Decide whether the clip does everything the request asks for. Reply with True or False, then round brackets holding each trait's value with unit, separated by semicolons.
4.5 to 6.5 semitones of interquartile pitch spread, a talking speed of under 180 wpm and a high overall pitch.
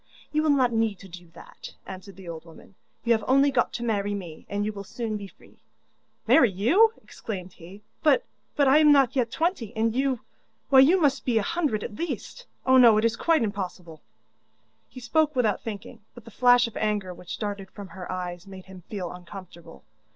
False (5.3 semitones; 205 wpm; 220 Hz)